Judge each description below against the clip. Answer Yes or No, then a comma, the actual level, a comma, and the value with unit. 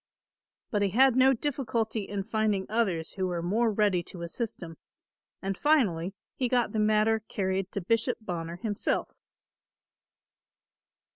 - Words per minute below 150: Yes, average, 140 wpm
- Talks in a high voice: Yes, high, 210 Hz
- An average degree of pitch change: Yes, average, 3.5 semitones